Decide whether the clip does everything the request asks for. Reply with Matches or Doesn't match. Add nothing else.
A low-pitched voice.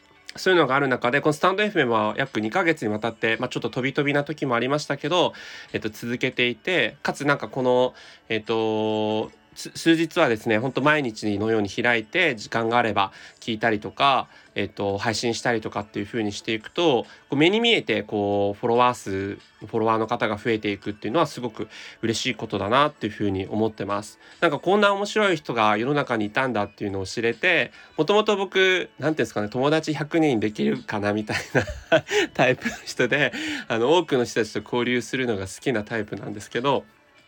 Matches